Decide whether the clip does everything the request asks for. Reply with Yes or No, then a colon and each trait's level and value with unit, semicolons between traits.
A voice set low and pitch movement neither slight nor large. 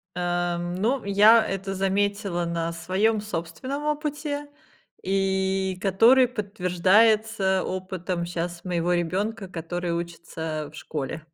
No: high, 190 Hz; average, 3.6 semitones